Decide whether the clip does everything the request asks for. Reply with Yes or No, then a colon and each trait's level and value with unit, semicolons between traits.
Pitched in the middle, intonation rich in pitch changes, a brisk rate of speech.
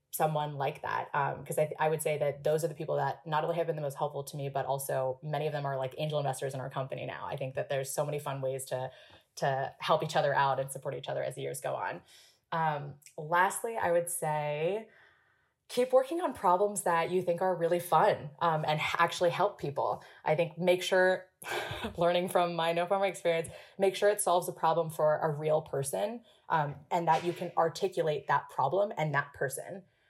No: medium, 160 Hz; average, 3.4 semitones; fast, 220 wpm